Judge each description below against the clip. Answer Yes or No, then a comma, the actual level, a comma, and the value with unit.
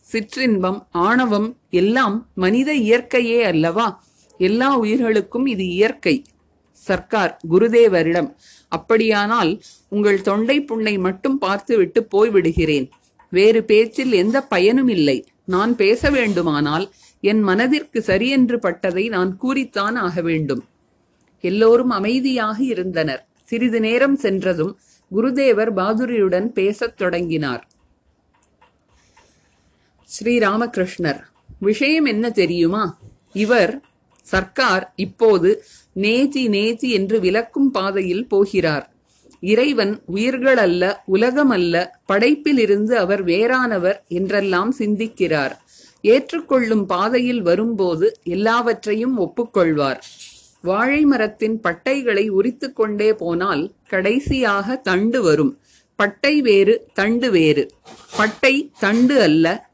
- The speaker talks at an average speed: Yes, average, 90 wpm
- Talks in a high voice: Yes, high, 215 Hz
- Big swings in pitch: No, average, 4.8 semitones